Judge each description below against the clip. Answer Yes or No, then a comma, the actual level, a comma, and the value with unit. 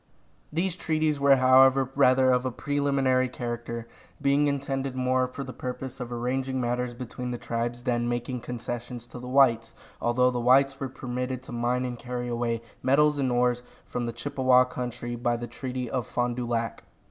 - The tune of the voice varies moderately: No, narrow, 1.7 semitones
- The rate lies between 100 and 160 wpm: No, average, 180 wpm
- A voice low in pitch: Yes, low, 125 Hz